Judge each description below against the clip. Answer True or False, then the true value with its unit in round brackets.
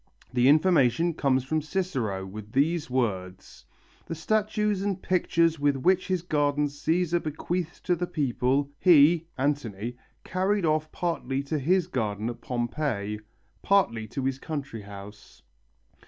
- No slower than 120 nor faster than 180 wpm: True (135 wpm)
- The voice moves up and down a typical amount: False (6.0 semitones)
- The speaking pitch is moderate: True (145 Hz)